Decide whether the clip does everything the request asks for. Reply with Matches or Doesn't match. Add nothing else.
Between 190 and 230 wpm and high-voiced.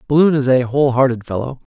Doesn't match